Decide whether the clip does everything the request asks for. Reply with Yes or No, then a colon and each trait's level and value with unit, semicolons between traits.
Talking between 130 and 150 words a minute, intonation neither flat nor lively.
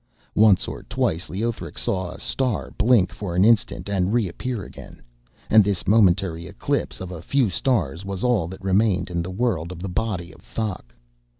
No: average, 180 wpm; average, 3.7 semitones